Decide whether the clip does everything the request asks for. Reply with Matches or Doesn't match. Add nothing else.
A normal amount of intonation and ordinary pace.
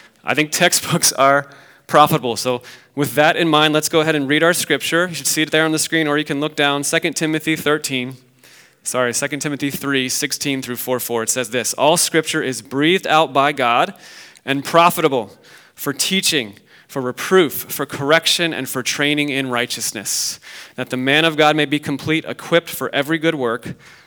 Matches